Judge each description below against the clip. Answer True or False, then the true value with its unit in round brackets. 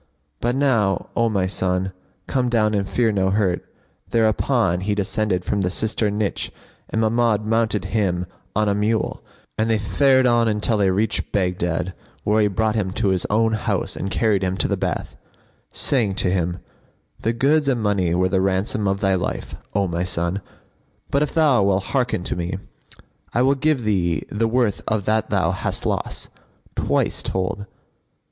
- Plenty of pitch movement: False (3.2 semitones)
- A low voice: True (105 Hz)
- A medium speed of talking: True (175 wpm)